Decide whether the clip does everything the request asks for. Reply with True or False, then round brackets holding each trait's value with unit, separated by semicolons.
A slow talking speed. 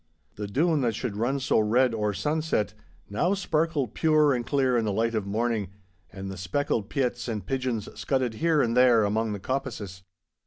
False (185 wpm)